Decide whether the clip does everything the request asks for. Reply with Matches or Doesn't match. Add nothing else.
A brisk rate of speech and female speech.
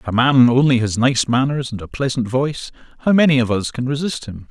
Doesn't match